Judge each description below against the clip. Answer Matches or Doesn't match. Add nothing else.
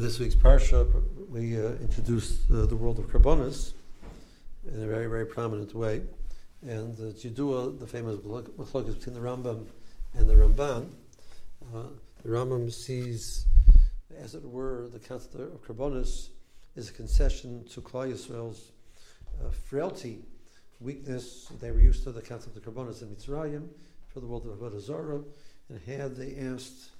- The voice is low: Matches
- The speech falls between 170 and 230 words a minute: Doesn't match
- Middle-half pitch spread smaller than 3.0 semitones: Matches